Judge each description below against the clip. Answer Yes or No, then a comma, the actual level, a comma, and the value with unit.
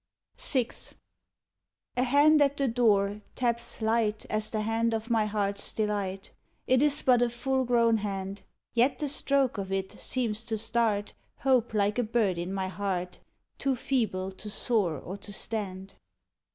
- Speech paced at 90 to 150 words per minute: No, average, 160 wpm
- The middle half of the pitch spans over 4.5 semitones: No, average, 3.5 semitones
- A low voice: No, high, 220 Hz